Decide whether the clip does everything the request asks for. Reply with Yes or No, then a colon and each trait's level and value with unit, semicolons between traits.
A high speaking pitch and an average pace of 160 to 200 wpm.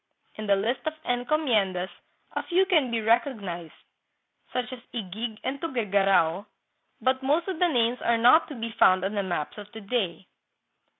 Yes: high, 230 Hz; average, 170 wpm